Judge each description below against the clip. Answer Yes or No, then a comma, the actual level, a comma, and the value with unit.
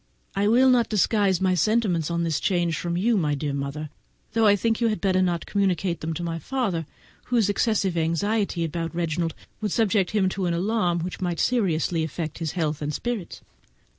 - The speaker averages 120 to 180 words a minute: No, average, 195 wpm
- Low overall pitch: No, medium, 180 Hz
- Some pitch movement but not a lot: Yes, average, 4.2 semitones